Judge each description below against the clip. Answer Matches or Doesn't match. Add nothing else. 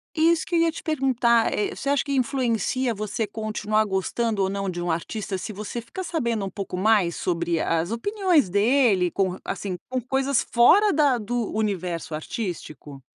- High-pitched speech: Matches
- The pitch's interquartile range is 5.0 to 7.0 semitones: Matches